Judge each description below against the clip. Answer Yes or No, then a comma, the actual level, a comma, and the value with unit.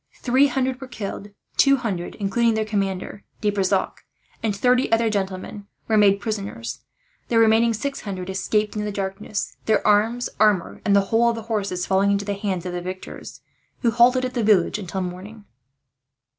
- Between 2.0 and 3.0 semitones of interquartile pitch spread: Yes, average, 2.7 semitones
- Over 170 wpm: Yes, average, 180 wpm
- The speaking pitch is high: Yes, high, 210 Hz